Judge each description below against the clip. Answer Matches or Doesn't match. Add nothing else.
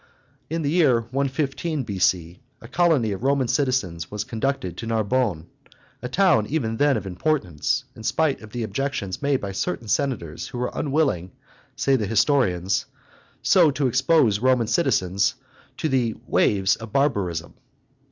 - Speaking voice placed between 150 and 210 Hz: Doesn't match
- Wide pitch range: Matches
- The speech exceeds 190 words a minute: Doesn't match